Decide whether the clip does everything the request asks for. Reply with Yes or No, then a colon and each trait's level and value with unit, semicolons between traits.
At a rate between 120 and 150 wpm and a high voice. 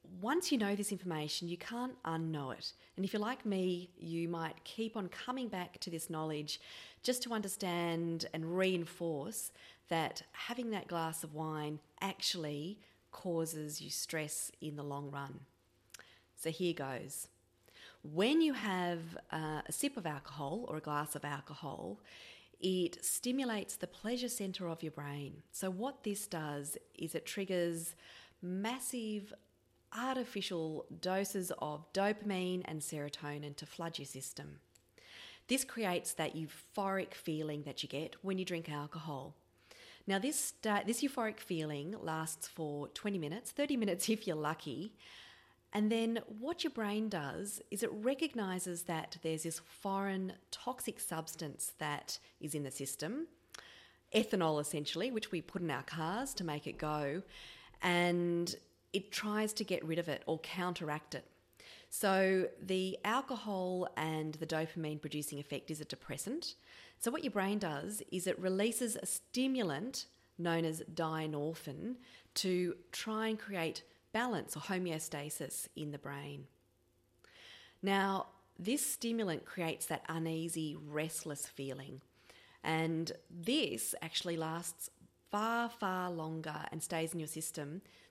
No: average, 140 wpm; medium, 175 Hz